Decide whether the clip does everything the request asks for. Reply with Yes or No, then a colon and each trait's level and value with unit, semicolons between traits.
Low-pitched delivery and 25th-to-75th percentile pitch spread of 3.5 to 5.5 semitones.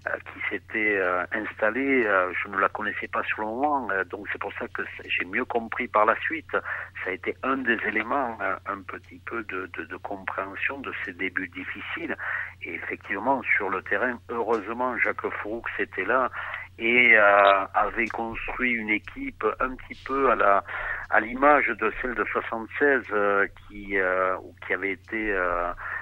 No: low, 110 Hz; average, 3.1 semitones